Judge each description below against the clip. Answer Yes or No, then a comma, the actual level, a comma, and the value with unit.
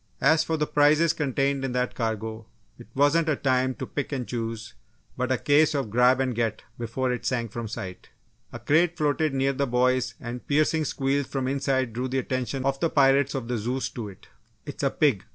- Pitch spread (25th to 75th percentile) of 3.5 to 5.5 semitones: No, average, 2.9 semitones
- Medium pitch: No, low, 130 Hz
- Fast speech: Yes, fast, 210 wpm